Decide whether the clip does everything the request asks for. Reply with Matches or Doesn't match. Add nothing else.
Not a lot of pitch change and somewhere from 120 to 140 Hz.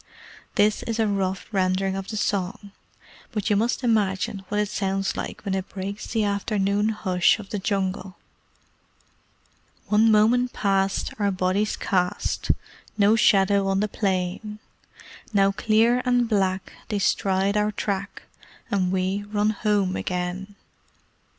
Doesn't match